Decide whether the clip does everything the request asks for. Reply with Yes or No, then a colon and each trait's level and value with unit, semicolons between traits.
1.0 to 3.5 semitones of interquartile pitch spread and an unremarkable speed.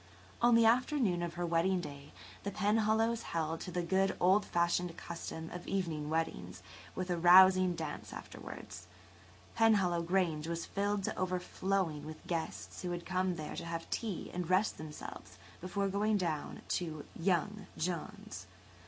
Yes: average, 3.2 semitones; average, 145 wpm